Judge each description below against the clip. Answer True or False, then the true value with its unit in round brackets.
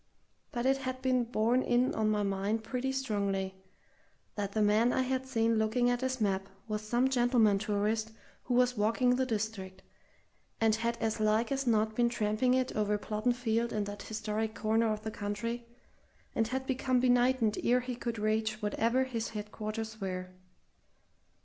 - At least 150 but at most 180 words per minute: True (170 wpm)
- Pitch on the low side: False (225 Hz)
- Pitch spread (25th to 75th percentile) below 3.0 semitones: True (2.6 semitones)